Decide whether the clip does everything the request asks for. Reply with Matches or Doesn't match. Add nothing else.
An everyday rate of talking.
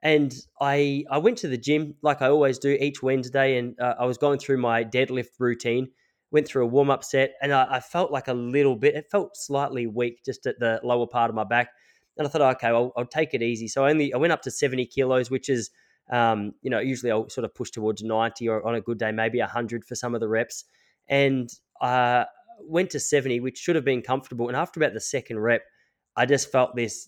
Doesn't match